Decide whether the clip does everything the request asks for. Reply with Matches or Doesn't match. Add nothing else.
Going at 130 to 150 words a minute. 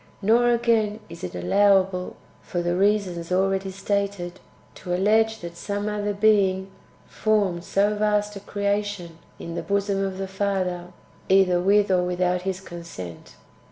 Matches